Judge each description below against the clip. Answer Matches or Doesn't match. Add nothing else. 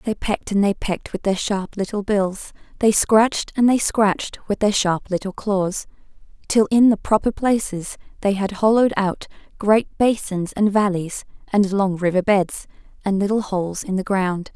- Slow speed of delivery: Doesn't match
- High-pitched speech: Matches